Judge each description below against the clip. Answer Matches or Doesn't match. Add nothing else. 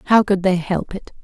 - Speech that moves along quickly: Matches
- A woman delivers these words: Matches